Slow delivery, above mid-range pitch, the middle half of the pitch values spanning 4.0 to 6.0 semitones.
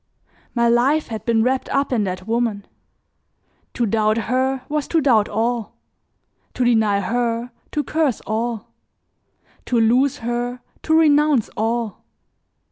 No: slow, 130 wpm; high, 240 Hz; average, 2.8 semitones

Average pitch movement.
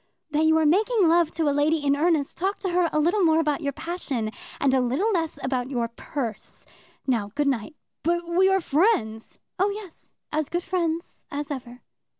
Yes: average, 4.1 semitones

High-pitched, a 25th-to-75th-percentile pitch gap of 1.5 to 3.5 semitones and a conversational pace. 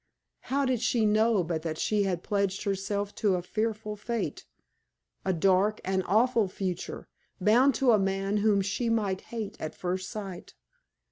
Yes: high, 205 Hz; narrow, 2.6 semitones; average, 160 wpm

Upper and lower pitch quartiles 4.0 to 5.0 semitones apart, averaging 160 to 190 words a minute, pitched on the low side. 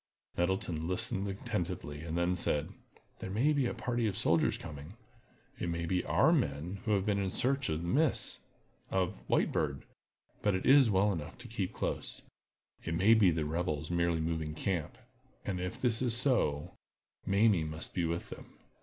Yes: average, 4.4 semitones; average, 175 wpm; very low, 90 Hz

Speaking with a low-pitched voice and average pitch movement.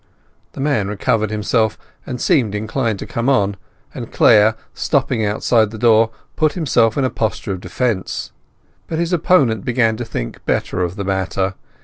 Yes: low, 110 Hz; average, 3.7 semitones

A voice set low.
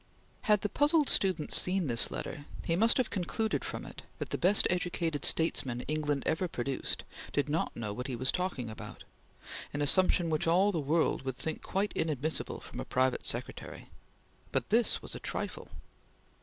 No: medium, 160 Hz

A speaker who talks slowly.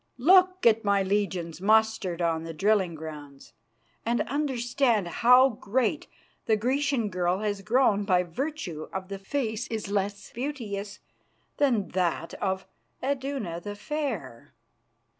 Yes: slow, 130 wpm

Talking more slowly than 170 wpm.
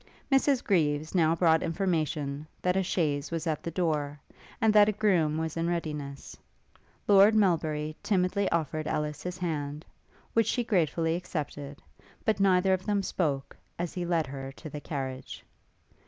Yes: average, 155 wpm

